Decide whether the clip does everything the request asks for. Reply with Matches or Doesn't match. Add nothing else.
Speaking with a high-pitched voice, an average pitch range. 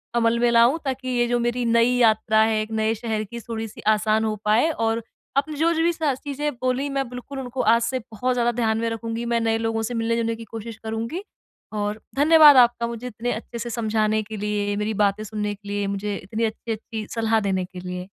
Doesn't match